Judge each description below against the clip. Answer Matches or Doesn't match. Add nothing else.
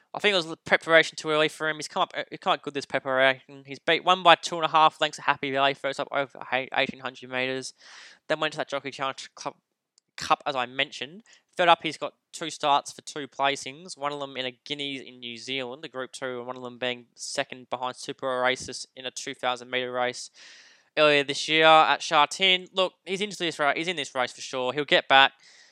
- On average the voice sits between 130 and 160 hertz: Matches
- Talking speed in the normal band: Doesn't match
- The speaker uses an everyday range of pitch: Matches